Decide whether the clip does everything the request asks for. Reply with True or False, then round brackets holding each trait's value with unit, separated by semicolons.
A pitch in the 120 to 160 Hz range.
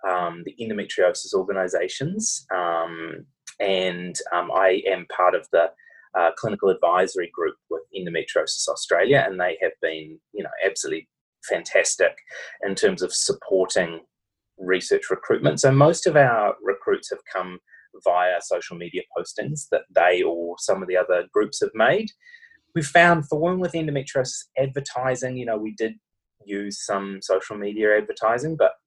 True (140 Hz)